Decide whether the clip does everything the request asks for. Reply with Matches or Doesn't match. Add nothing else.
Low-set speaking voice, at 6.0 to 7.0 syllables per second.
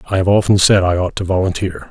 Matches